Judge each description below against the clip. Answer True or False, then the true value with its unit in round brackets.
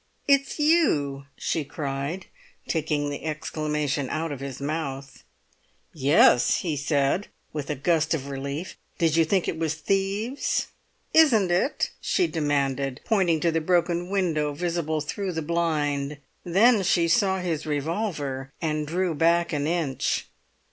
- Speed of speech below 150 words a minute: True (140 wpm)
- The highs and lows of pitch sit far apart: False (3.6 semitones)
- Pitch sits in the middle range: True (160 Hz)